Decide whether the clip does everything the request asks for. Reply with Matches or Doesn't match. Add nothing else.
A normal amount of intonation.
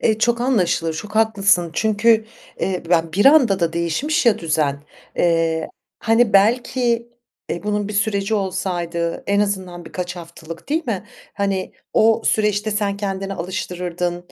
Matches